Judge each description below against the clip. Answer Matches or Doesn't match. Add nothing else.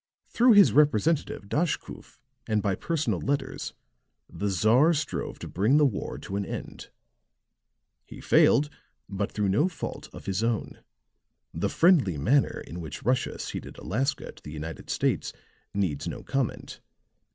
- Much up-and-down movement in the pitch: Matches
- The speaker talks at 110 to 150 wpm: Matches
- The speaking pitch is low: Matches